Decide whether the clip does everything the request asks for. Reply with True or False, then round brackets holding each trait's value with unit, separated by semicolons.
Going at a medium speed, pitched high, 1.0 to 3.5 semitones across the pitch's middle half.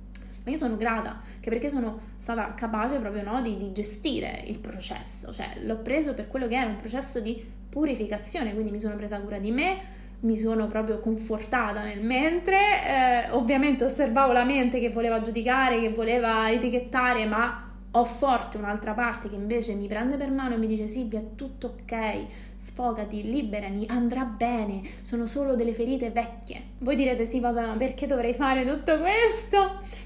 False (175 wpm; 235 Hz; 2.9 semitones)